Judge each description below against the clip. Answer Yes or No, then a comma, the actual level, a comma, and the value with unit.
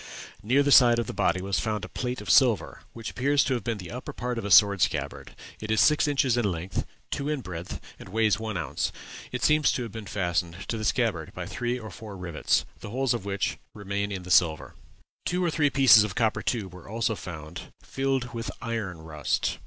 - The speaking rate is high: Yes, fast, 225 wpm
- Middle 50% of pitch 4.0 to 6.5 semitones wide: Yes, average, 4.7 semitones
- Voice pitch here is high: No, low, 110 Hz